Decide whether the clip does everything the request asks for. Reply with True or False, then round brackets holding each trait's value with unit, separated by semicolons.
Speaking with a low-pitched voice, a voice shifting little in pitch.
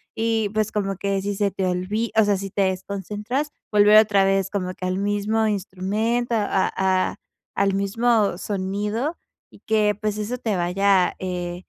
False (200 Hz; 2.0 semitones)